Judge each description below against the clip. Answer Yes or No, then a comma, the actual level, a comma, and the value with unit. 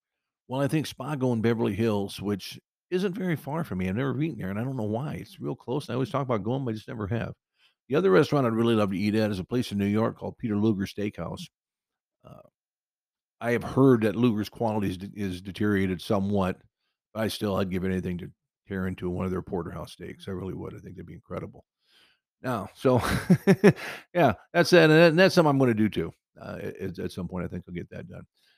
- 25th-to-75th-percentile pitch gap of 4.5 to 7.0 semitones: Yes, average, 5.3 semitones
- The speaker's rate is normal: No, fast, 235 wpm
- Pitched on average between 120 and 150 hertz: No, low, 110 Hz